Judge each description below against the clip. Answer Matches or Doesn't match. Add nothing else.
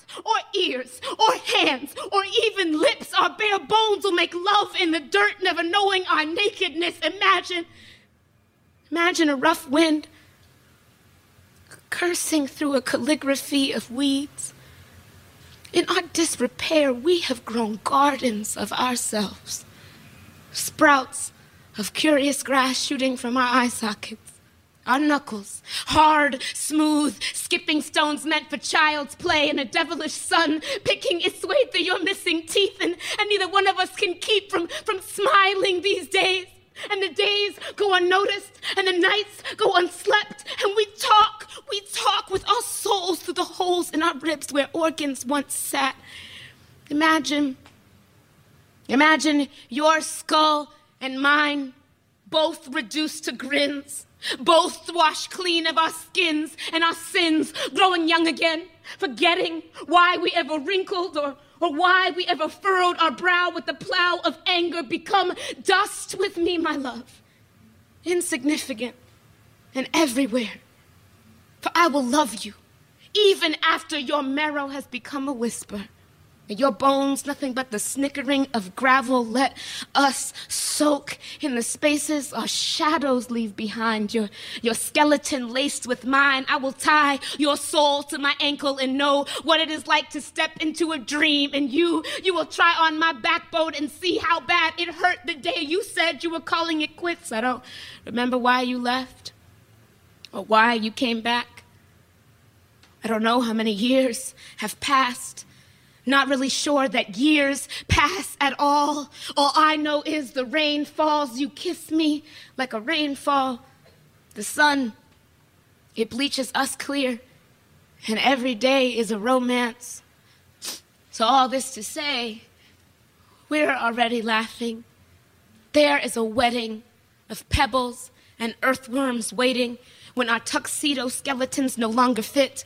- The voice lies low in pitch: Doesn't match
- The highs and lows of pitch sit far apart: Doesn't match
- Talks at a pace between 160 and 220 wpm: Doesn't match